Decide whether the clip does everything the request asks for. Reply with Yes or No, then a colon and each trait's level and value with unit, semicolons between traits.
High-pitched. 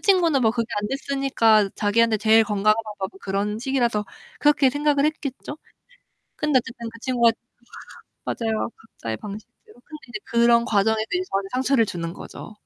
Yes: high, 230 Hz